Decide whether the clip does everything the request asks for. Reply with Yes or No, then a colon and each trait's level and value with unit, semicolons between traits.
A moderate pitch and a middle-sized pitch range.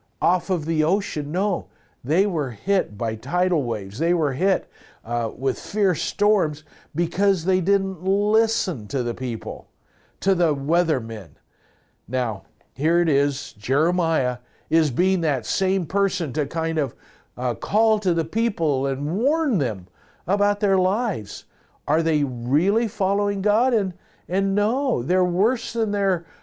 No: medium, 175 Hz; wide, 5.8 semitones